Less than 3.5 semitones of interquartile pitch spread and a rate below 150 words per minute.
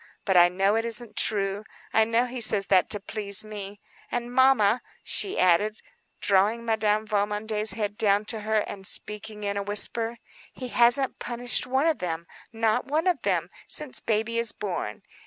No: narrow, 2.6 semitones; average, 165 wpm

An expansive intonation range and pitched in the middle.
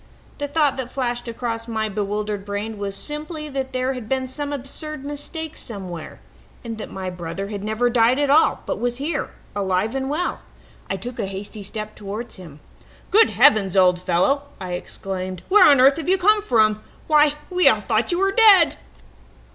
No: wide, 6.2 semitones; high, 235 Hz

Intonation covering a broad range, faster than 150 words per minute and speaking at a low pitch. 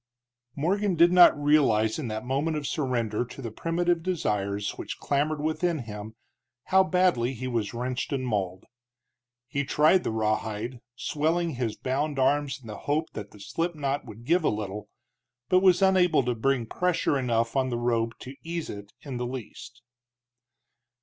Yes: wide, 5.8 semitones; average, 165 wpm; low, 130 Hz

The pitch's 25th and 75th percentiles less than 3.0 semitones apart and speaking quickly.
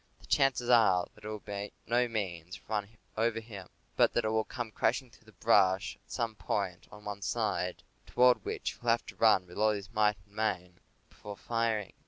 Yes: narrow, 2.5 semitones; fast, 210 wpm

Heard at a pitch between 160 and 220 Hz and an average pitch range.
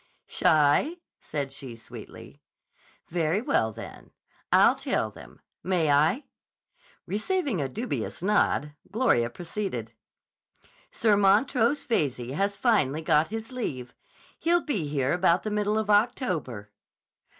No: medium, 185 Hz; wide, 7.4 semitones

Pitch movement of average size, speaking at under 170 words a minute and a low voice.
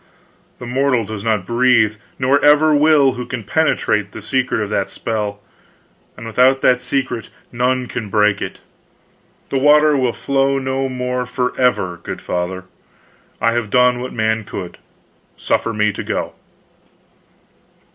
Yes: average, 3.5 semitones; average, 145 wpm; low, 125 Hz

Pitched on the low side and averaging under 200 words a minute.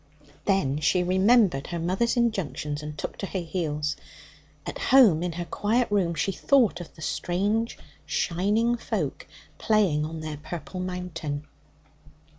No: medium, 180 Hz; average, 140 wpm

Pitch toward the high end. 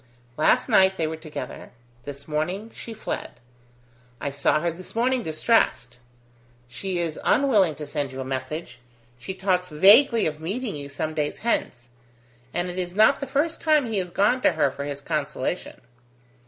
No: medium, 175 Hz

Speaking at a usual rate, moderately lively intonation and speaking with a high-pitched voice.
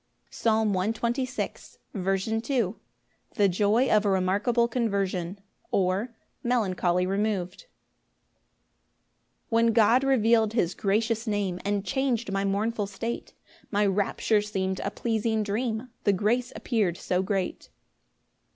No: slow, 115 wpm; average, 3.1 semitones; high, 210 Hz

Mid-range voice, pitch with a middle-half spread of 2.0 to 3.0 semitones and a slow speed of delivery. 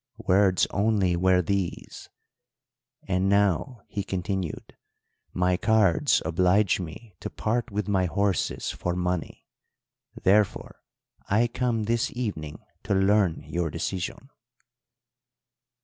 No: very low, 95 Hz; average, 2.7 semitones; slow, 105 wpm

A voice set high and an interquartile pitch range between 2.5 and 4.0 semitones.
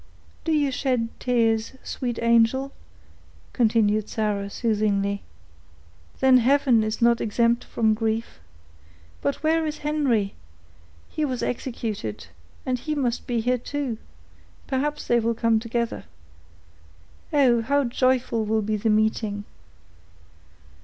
Yes: high, 235 Hz; average, 3.1 semitones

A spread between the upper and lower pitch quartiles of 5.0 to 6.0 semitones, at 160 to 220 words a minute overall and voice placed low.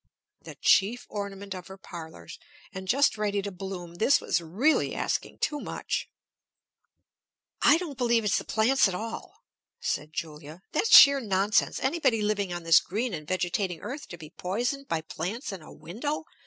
No: wide, 5.6 semitones; average, 170 wpm; high, 200 Hz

